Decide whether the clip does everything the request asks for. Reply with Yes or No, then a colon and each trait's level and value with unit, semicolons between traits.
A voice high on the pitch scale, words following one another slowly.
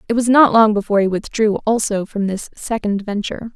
No: high, 215 Hz; fast, 205 wpm